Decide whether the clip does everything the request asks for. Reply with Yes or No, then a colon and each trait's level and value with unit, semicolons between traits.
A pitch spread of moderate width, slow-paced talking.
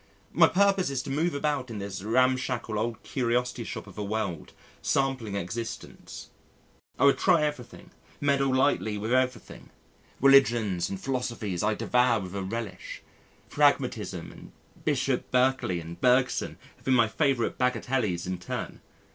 No: average, 4.3 semitones; average, 145 wpm